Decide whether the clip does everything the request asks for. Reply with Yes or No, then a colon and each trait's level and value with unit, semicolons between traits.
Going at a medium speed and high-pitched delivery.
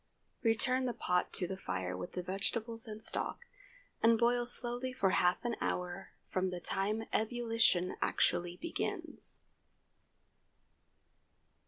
No: slow, 125 wpm; high, 215 Hz